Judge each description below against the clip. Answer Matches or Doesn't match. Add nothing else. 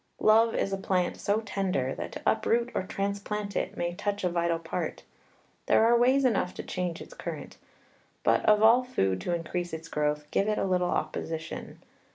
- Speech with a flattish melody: Doesn't match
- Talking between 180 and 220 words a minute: Matches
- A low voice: Doesn't match